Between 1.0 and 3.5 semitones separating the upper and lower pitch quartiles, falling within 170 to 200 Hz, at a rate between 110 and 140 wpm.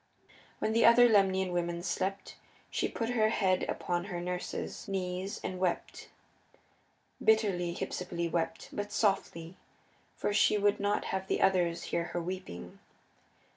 Yes: average, 2.7 semitones; medium, 185 Hz; slow, 135 wpm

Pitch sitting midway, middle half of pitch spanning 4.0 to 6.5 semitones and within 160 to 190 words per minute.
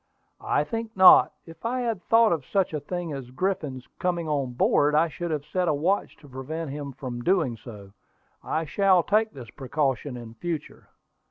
Yes: medium, 155 Hz; wide, 5.5 semitones; average, 185 wpm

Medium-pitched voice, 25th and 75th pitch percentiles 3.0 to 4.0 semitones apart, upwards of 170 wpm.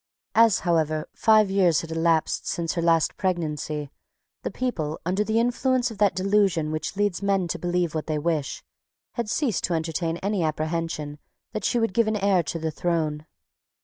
No: medium, 175 Hz; average, 4.4 semitones; average, 180 wpm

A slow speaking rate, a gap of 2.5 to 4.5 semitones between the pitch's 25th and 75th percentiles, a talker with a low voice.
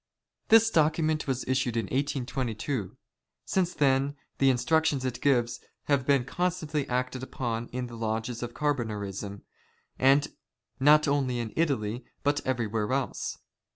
Yes: slow, 130 wpm; average, 3.5 semitones; low, 130 Hz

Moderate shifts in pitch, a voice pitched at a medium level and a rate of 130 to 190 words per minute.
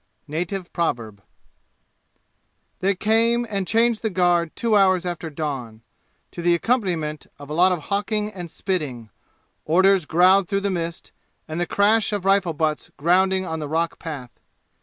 Yes: average, 3.9 semitones; medium, 180 Hz; average, 155 wpm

